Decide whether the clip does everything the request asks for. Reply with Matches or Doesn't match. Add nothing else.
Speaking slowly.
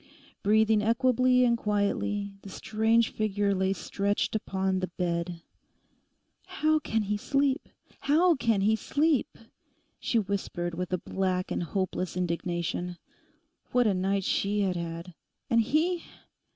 Matches